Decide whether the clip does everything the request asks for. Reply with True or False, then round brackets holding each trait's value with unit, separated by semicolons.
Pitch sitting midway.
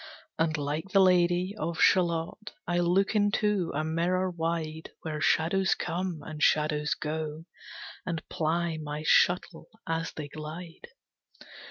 True (165 Hz)